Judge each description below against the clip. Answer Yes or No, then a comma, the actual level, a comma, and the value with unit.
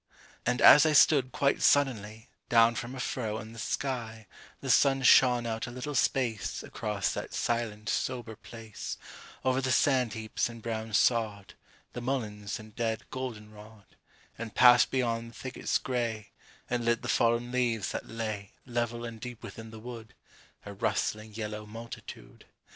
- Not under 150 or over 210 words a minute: Yes, average, 160 wpm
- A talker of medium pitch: No, low, 115 Hz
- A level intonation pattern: Yes, narrow, 2.2 semitones